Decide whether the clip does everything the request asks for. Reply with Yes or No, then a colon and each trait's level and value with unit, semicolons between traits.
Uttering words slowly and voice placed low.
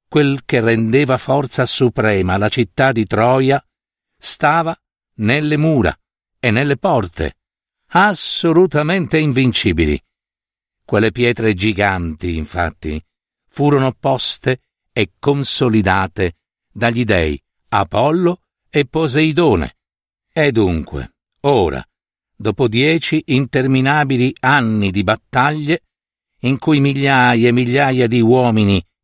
Yes: slow, 95 wpm; low, 125 Hz